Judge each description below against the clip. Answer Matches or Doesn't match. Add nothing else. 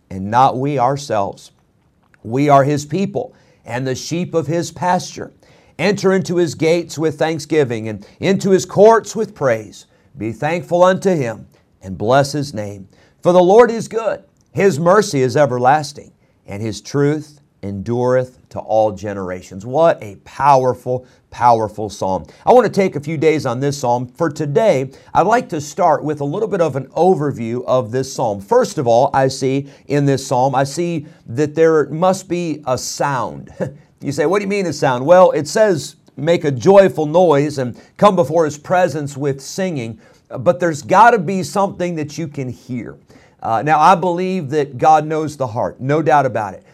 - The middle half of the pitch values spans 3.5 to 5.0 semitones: Doesn't match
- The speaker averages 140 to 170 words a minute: Doesn't match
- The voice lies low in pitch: Doesn't match